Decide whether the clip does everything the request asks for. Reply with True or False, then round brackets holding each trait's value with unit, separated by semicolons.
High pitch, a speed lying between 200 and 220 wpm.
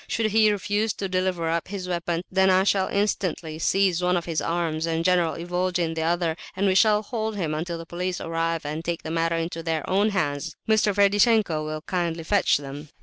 False (175 Hz; 205 wpm)